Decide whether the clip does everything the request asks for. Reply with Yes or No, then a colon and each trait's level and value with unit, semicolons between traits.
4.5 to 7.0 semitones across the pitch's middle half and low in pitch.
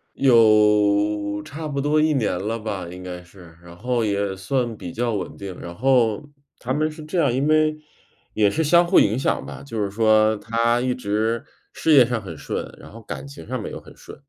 Yes: average, 4.8 semitones; low, 115 Hz